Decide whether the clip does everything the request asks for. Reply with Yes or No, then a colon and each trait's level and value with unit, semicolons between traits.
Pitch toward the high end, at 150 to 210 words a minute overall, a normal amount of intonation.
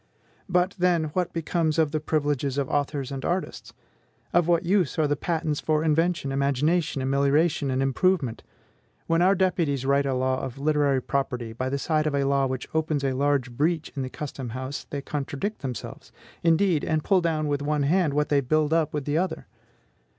No: medium, 150 Hz; average, 190 wpm; average, 3.1 semitones